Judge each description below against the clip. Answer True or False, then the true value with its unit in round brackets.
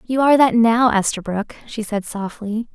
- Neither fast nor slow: True (175 wpm)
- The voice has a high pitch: True (225 Hz)